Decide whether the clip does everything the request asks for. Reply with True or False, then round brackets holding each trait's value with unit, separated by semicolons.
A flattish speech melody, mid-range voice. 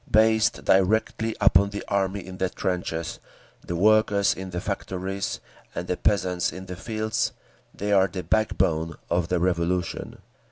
False (2.3 semitones; 95 Hz)